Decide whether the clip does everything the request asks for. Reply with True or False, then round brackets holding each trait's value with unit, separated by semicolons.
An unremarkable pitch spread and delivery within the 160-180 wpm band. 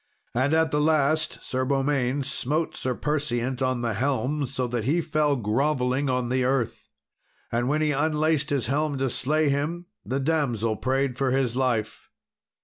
True (3.0 semitones; 165 wpm)